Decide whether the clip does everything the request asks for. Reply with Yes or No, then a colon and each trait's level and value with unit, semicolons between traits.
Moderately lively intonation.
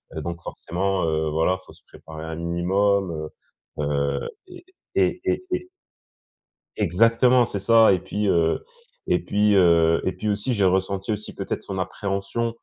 Yes: average, 3.9 semitones